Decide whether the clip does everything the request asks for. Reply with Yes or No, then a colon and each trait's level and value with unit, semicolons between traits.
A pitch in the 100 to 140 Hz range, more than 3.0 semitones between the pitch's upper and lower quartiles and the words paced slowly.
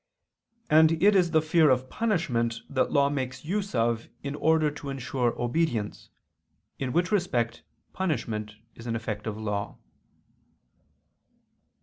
Yes: low, 135 Hz; wide, 5.6 semitones; slow, 130 wpm